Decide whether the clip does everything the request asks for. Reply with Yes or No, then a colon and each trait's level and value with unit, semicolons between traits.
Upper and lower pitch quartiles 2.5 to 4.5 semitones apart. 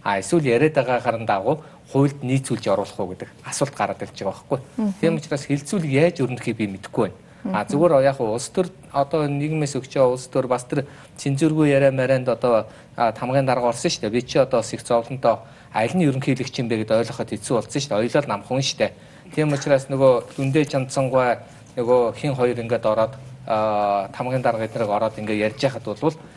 Yes: average, 3.2 semitones